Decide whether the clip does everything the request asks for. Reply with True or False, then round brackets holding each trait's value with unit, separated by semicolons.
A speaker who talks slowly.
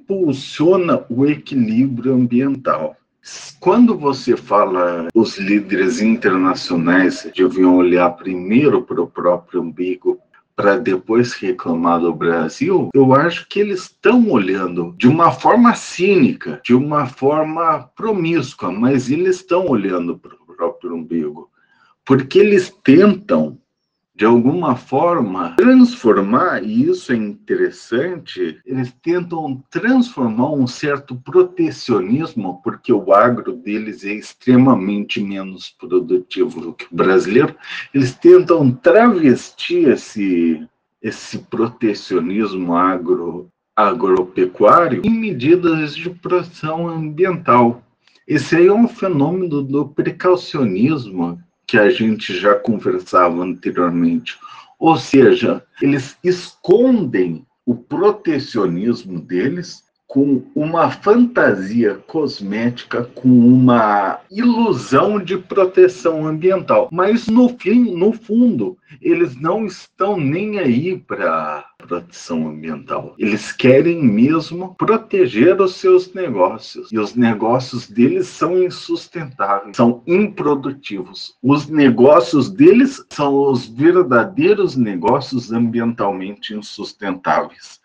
True (105 wpm)